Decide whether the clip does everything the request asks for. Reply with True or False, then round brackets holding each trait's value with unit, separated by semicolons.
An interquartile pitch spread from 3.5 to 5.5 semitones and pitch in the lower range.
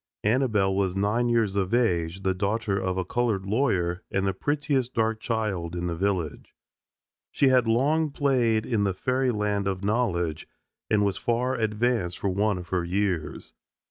True (4.1 semitones; 105 Hz)